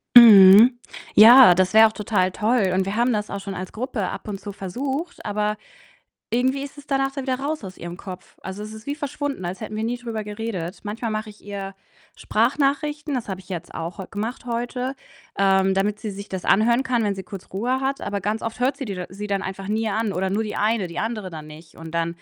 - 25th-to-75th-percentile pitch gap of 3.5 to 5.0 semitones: Yes, average, 4.1 semitones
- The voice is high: Yes, high, 210 Hz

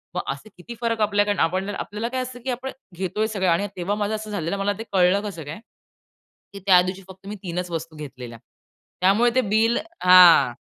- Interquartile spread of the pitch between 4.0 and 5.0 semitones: No, average, 3.3 semitones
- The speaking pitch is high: Yes, high, 195 Hz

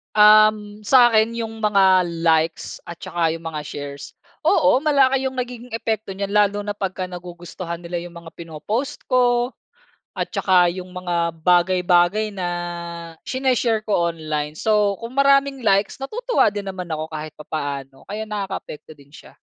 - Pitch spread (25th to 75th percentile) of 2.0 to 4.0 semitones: No, average, 4.7 semitones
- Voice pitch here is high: Yes, high, 195 Hz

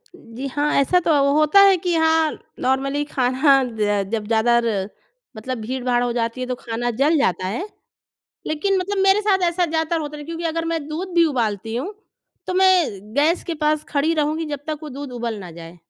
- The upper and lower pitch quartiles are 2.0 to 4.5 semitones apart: No, wide, 5.5 semitones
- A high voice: Yes, very high, 290 Hz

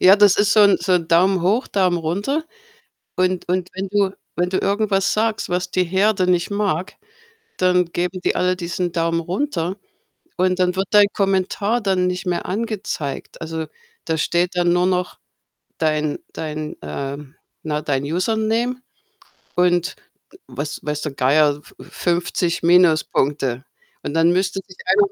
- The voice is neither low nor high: Yes, medium, 180 Hz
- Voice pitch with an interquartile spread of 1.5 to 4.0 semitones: Yes, average, 2.9 semitones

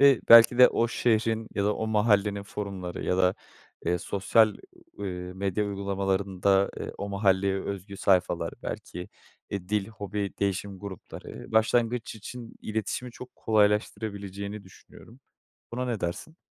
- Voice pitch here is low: Yes, low, 100 Hz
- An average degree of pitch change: No, narrow, 2.2 semitones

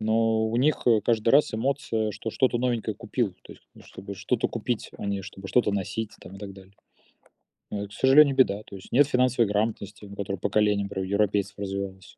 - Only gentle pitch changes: No, average, 3.1 semitones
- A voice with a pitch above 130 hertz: No, low, 105 Hz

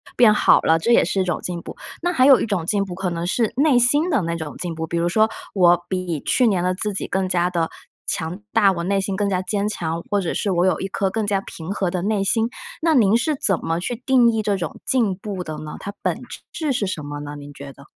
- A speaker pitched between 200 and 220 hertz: No, high, 190 Hz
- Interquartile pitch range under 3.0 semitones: No, average, 4.1 semitones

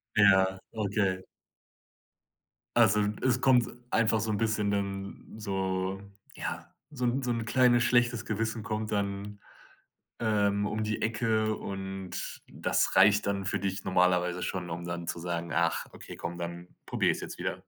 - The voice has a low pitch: Yes, low, 100 Hz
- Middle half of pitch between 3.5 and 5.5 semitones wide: No, average, 2.7 semitones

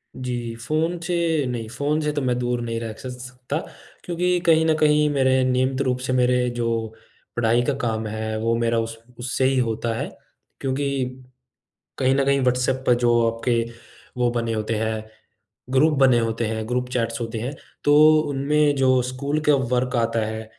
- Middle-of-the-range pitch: No, low, 125 Hz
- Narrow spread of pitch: No, average, 3.1 semitones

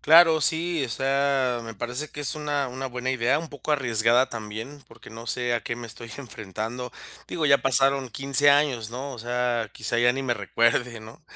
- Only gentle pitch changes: No, average, 3.1 semitones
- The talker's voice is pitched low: Yes, low, 125 Hz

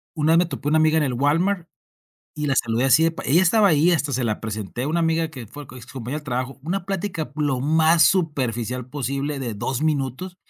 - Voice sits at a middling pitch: Yes, medium, 150 Hz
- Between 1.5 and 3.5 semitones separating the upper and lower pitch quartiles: No, average, 4.2 semitones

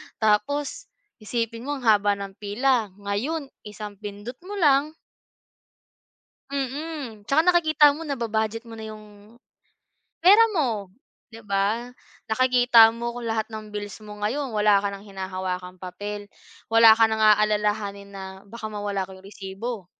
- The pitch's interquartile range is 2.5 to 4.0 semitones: Yes, average, 3.5 semitones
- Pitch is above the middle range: Yes, high, 220 Hz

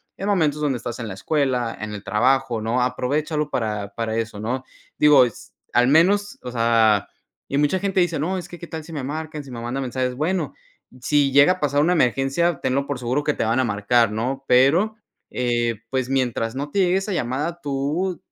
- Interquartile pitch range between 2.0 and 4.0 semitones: No, average, 4.5 semitones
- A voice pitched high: No, low, 135 Hz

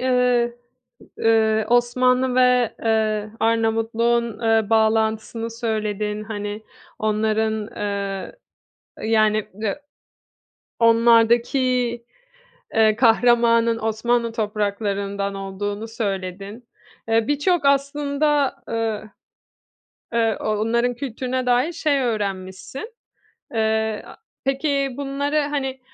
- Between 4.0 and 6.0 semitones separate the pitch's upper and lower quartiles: No, narrow, 2.6 semitones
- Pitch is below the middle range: No, high, 225 Hz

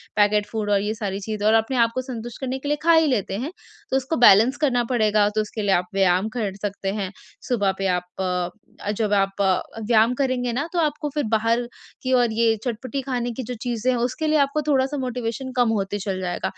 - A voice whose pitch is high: Yes, high, 230 Hz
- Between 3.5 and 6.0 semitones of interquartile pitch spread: Yes, average, 3.9 semitones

